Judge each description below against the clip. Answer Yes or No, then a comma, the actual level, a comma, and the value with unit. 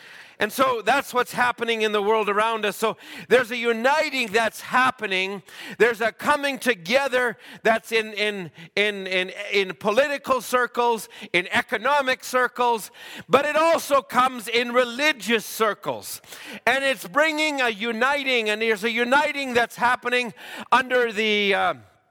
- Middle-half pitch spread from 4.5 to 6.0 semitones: No, average, 3.1 semitones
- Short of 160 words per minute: Yes, average, 140 wpm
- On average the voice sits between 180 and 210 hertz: No, high, 240 Hz